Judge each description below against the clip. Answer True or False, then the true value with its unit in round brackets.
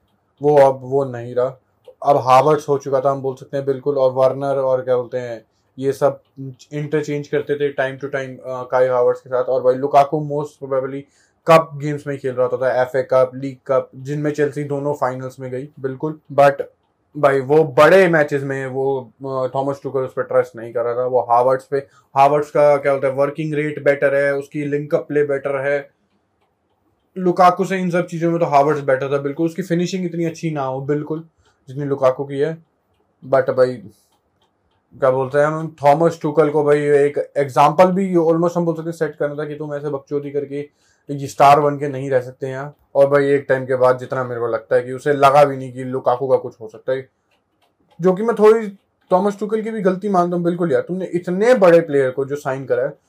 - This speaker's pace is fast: True (215 wpm)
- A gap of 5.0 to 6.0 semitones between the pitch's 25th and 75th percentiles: False (2.6 semitones)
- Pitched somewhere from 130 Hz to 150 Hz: True (140 Hz)